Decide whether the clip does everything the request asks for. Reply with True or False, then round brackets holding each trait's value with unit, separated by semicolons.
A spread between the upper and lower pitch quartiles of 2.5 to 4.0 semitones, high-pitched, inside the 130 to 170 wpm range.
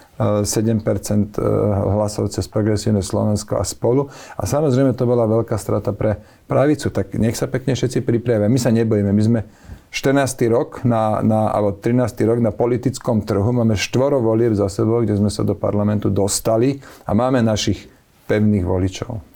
False (2.8 semitones; 110 Hz; 160 wpm)